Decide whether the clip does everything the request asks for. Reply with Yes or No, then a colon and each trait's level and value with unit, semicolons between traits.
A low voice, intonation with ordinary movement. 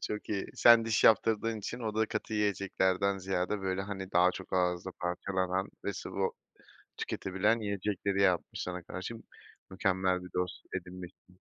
No: very low, 95 Hz; narrow, 2.1 semitones